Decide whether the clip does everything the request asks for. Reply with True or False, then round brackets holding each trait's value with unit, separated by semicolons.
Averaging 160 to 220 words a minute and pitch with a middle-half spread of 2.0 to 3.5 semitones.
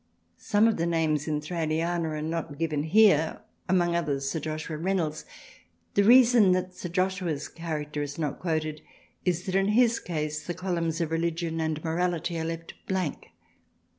True (165 wpm; 2.7 semitones)